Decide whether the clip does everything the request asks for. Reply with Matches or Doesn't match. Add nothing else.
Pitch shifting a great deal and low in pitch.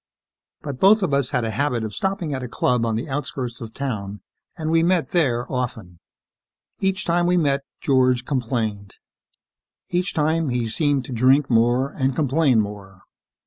Doesn't match